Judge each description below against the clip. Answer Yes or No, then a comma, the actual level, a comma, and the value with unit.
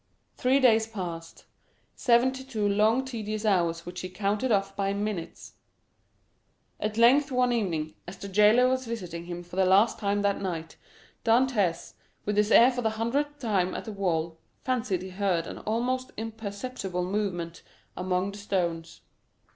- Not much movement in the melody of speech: No, average, 4.3 semitones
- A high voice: Yes, high, 205 Hz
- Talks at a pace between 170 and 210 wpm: No, average, 155 wpm